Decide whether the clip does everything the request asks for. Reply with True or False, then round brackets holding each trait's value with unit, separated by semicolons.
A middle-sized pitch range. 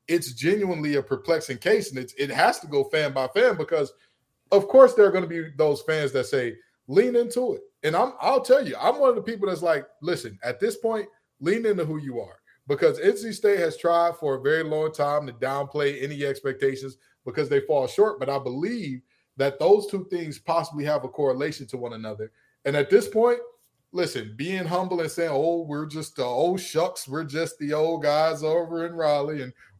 False (7.3 semitones)